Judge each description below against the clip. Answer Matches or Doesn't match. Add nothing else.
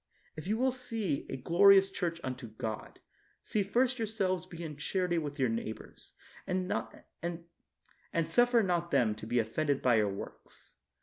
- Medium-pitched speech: Matches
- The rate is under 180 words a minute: Matches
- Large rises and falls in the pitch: Matches